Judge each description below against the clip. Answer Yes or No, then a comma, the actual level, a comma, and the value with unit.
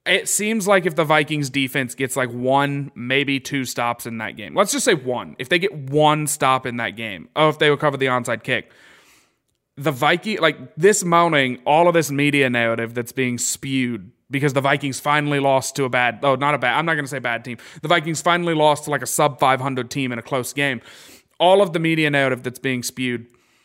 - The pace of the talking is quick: Yes, fast, 225 wpm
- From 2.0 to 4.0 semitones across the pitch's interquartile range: Yes, average, 3.5 semitones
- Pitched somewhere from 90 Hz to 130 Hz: No, medium, 140 Hz